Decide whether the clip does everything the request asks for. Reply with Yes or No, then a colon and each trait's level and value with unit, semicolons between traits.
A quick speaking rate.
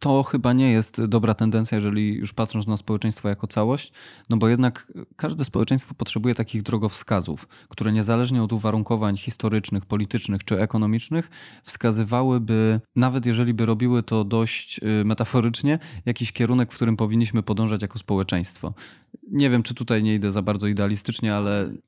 No: average, 150 wpm